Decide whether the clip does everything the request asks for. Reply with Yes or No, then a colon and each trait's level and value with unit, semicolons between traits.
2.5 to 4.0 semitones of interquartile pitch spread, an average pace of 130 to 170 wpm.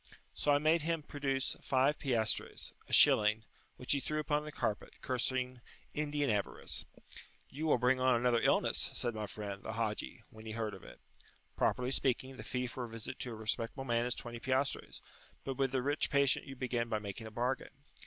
No: average, 3.1 semitones; average, 195 wpm